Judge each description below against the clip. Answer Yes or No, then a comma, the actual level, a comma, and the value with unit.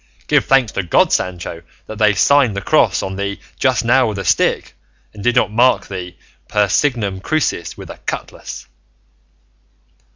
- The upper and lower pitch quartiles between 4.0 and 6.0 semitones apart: Yes, average, 4.4 semitones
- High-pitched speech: No, low, 105 Hz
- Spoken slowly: No, average, 165 wpm